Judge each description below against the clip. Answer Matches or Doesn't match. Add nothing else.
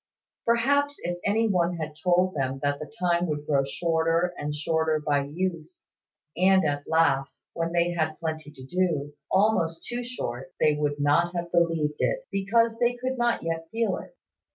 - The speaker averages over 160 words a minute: Matches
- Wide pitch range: Doesn't match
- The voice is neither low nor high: Matches